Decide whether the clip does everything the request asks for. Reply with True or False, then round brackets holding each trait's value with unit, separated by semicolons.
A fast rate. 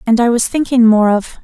True (250 wpm)